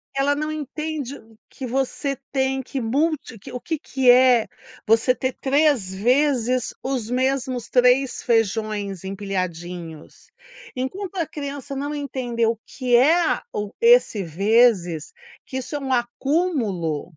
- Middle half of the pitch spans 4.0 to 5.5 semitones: Yes, average, 4.3 semitones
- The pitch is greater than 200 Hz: Yes, very high, 255 Hz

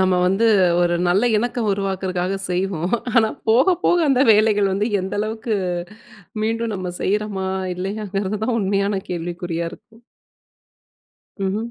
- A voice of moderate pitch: No, high, 200 Hz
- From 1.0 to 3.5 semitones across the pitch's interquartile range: Yes, average, 2.9 semitones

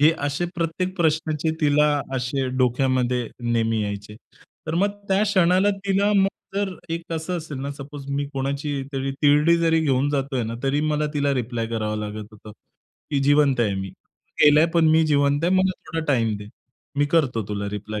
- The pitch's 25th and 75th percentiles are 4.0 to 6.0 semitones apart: Yes, average, 4.9 semitones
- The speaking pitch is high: No, medium, 145 Hz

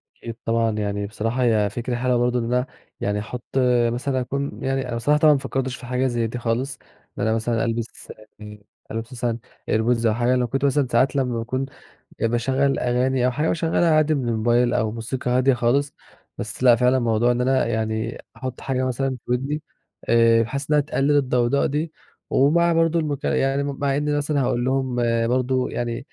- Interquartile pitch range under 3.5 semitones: Yes, average, 2.7 semitones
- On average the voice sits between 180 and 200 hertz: No, low, 125 Hz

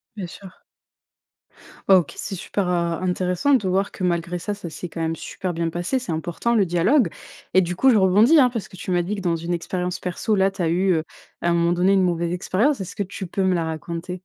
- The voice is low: No, medium, 180 Hz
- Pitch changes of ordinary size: No, narrow, 2.3 semitones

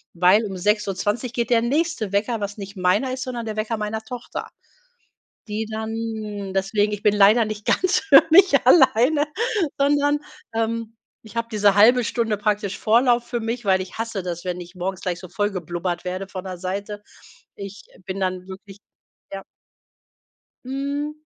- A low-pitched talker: No, high, 210 Hz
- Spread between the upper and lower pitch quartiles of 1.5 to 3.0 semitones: No, average, 3.4 semitones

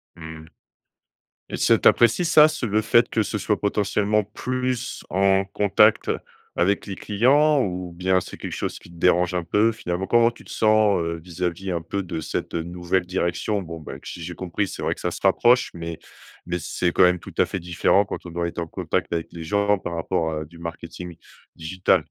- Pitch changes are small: No, average, 3.6 semitones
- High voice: No, very low, 90 Hz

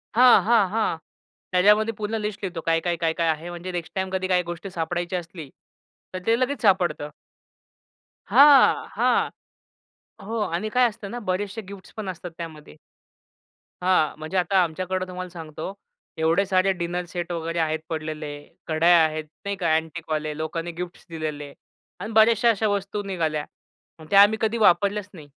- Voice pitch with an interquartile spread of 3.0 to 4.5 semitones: Yes, average, 3.8 semitones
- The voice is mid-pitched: Yes, medium, 180 Hz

